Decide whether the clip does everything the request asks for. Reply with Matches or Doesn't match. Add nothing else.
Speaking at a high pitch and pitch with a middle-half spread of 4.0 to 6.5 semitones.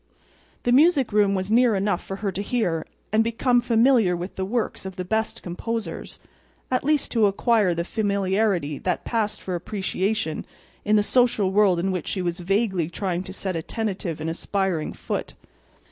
Doesn't match